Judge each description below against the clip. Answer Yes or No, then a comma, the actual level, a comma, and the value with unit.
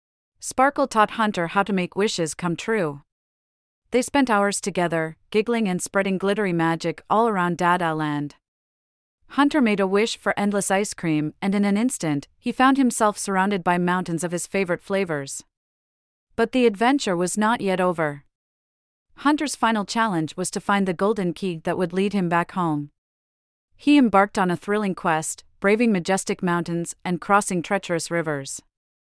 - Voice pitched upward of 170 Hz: Yes, medium, 185 Hz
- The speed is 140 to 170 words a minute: Yes, average, 165 wpm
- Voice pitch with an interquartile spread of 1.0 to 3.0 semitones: No, average, 4.5 semitones